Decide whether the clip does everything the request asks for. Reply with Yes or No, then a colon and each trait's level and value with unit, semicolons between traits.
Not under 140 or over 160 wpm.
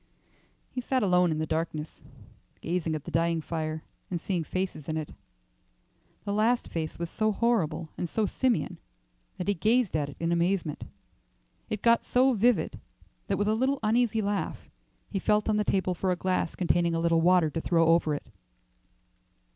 No: average, 180 wpm